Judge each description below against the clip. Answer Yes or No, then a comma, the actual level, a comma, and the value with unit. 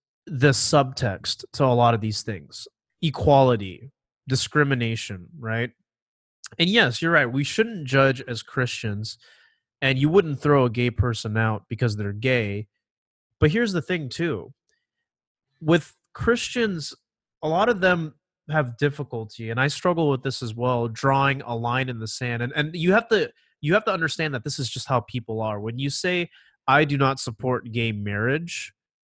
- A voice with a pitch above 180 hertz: No, low, 130 Hz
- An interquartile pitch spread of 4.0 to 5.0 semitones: Yes, average, 4.7 semitones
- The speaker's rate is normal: Yes, average, 170 wpm